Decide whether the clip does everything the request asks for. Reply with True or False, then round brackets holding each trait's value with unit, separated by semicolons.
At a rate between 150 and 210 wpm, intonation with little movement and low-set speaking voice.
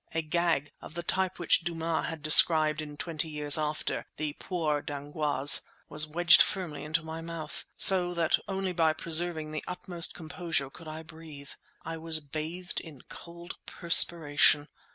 False (155 wpm; 2.0 semitones; 160 Hz)